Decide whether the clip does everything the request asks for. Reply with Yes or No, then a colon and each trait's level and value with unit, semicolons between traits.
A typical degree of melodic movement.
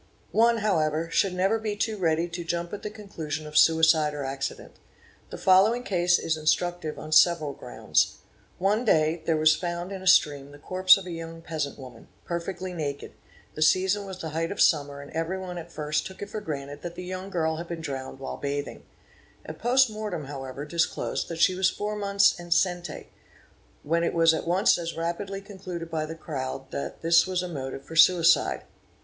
Yes: average, 3.3 semitones